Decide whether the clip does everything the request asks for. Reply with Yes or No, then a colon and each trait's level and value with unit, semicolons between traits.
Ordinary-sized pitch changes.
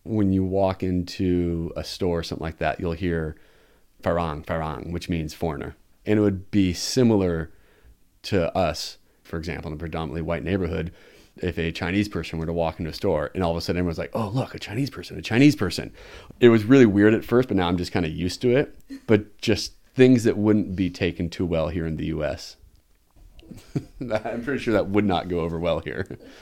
Yes: average, 3.8 semitones